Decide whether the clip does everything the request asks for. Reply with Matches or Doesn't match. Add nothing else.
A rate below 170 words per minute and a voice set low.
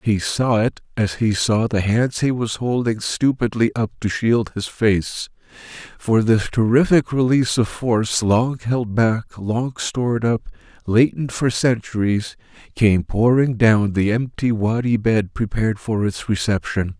Matches